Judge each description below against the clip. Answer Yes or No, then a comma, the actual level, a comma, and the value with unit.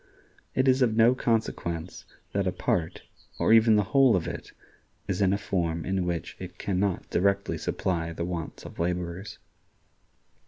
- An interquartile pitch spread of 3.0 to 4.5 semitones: Yes, average, 4.0 semitones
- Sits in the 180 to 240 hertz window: No, very low, 95 Hz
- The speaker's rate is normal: Yes, average, 165 wpm